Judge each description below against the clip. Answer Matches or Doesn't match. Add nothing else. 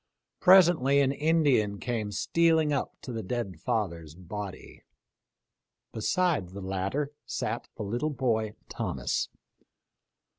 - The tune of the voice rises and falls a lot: Matches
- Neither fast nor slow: Doesn't match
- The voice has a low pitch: Matches